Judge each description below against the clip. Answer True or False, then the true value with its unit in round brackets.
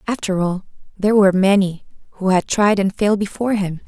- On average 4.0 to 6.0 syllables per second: False (6.3 syllables/s)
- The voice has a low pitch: False (195 Hz)